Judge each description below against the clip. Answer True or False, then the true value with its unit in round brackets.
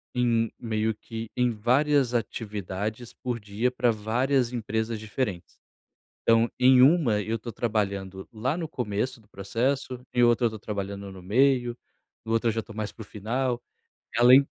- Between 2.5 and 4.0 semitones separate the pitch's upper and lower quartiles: True (2.9 semitones)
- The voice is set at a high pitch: False (115 Hz)